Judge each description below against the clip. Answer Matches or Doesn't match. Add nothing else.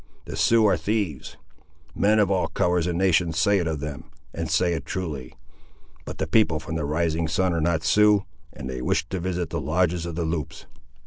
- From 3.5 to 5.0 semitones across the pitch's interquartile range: Doesn't match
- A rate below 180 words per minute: Doesn't match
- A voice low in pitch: Matches